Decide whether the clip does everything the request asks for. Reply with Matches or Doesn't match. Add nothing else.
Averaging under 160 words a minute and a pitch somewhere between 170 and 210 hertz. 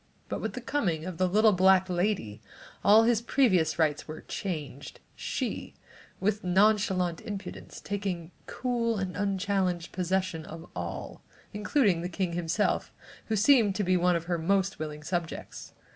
Matches